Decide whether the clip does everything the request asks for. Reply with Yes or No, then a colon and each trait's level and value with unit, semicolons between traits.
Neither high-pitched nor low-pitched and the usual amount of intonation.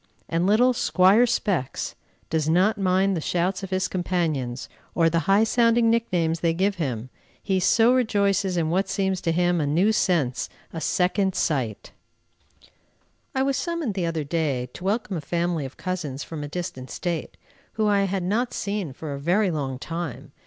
Yes: medium, 180 Hz; average, 3.9 semitones